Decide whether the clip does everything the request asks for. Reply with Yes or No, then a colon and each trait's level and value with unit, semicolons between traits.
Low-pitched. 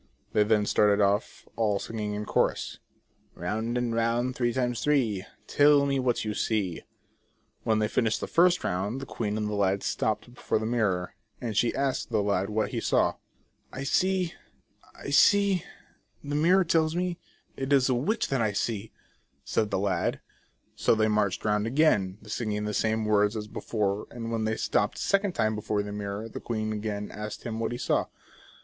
Yes: low, 110 Hz